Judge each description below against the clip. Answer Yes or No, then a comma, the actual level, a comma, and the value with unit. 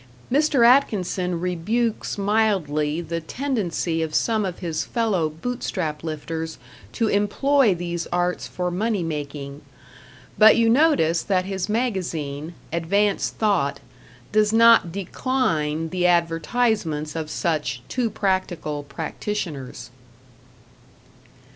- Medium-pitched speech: Yes, medium, 180 Hz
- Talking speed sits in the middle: No, slow, 105 wpm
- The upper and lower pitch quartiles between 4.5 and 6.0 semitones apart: Yes, average, 5.2 semitones